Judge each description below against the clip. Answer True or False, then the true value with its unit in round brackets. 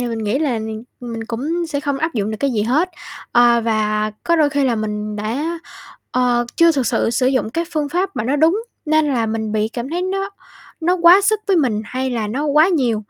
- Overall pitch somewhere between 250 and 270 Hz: True (255 Hz)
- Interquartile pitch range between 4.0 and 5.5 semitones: False (6.1 semitones)